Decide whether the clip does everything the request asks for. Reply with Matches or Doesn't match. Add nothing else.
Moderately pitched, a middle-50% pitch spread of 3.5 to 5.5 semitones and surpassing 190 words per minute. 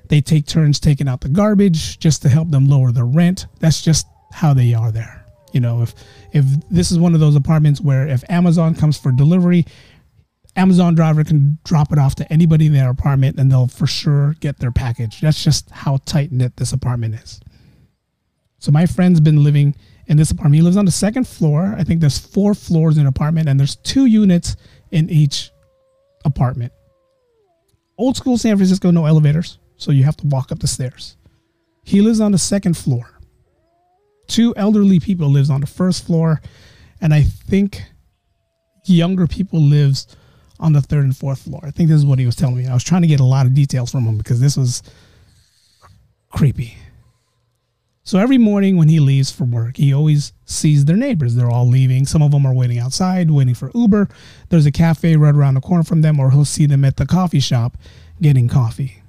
Matches